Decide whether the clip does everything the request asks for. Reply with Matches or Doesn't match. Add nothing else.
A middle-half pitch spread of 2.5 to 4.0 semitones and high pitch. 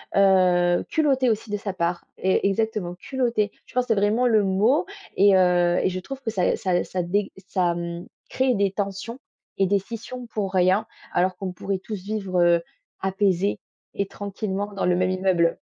Matches